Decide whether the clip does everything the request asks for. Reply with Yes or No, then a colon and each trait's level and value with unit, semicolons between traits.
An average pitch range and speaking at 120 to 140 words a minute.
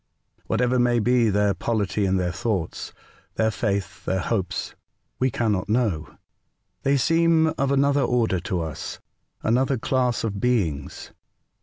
Yes: average, 4.8 semitones; slow, 135 wpm